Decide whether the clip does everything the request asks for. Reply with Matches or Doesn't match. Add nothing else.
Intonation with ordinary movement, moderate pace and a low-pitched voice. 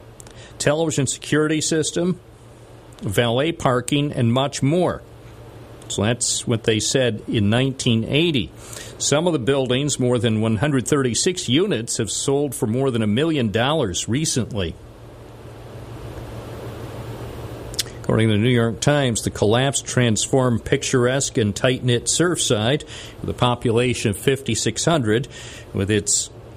Doesn't match